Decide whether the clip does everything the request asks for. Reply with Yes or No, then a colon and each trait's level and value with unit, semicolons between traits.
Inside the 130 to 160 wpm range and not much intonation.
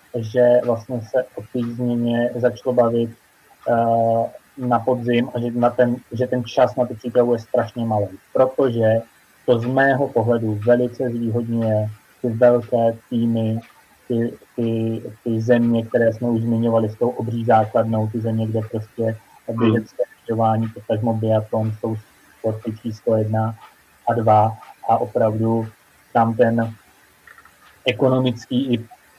Yes: average, 140 wpm; narrow, 1.5 semitones